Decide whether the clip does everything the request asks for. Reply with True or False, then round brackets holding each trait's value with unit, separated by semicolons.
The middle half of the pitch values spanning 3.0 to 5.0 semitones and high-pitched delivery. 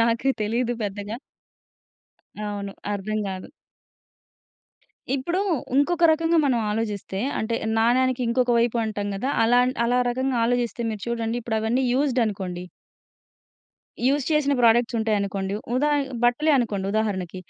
True (3.6 semitones; 235 Hz)